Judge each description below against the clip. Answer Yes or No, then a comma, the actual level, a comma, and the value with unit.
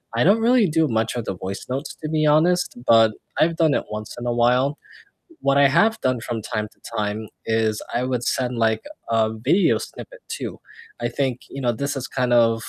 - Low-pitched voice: Yes, low, 125 Hz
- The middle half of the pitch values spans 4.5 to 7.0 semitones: Yes, average, 4.9 semitones